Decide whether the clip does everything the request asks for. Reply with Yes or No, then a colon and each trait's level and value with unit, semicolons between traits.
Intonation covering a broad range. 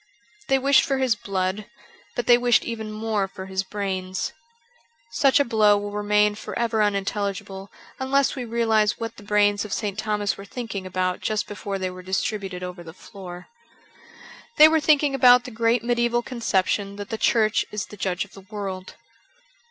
No: average, 3.4 semitones